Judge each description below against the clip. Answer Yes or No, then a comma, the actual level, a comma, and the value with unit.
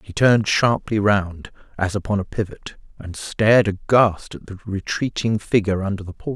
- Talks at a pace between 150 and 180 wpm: Yes, average, 170 wpm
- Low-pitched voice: Yes, low, 105 Hz